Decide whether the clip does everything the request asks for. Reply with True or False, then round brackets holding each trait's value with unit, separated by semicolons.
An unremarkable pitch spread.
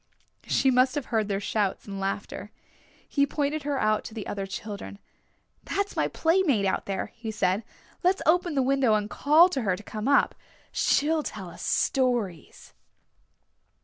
False (6.1 semitones)